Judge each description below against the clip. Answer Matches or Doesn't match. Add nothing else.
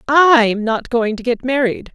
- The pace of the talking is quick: Doesn't match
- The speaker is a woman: Matches